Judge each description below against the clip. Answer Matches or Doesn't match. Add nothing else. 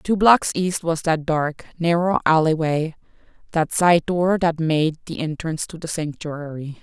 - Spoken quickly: Doesn't match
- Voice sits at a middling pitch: Matches